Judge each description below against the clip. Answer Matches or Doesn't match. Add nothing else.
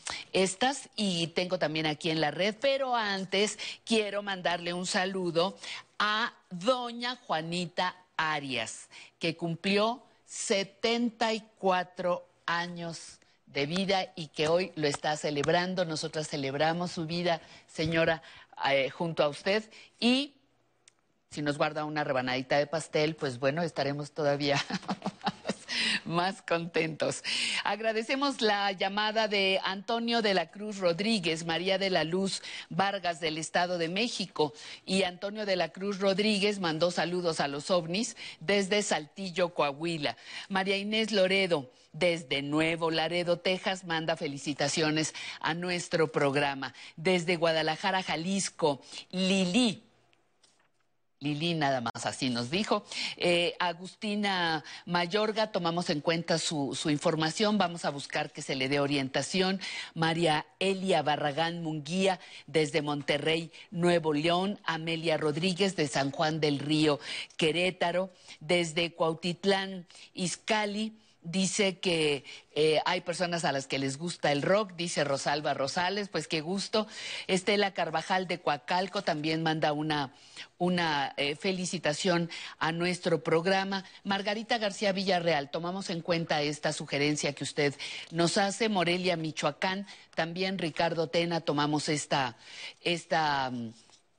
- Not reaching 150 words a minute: Matches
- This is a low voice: Doesn't match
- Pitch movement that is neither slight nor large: Matches